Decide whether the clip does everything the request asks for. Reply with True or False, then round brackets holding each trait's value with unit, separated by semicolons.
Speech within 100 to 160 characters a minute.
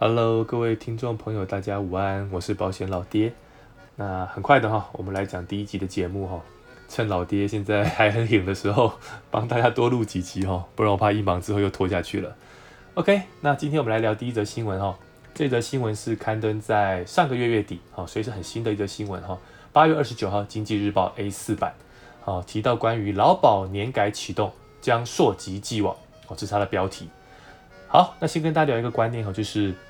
False (320 characters per minute)